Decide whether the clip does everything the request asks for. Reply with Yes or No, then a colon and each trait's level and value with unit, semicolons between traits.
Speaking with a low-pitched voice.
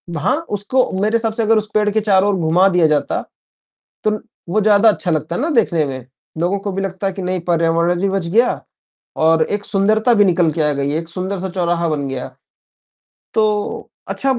No: high, 190 Hz